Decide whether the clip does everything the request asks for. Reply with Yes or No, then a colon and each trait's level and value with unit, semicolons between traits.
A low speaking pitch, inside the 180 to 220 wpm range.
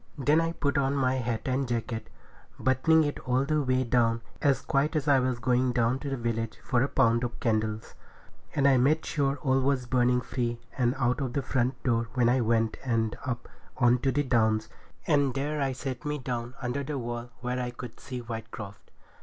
Yes: low, 125 Hz; fast, 205 wpm